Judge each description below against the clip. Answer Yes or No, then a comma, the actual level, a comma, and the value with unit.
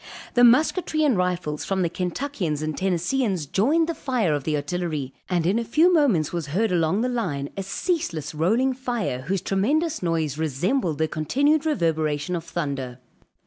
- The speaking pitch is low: No, medium, 180 Hz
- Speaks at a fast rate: No, average, 170 wpm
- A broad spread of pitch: Yes, wide, 8.2 semitones